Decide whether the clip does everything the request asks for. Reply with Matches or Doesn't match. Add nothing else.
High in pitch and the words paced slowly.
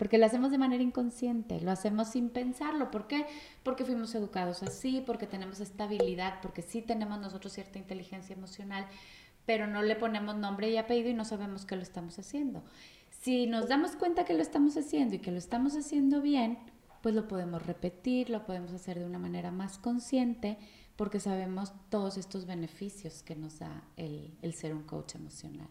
Doesn't match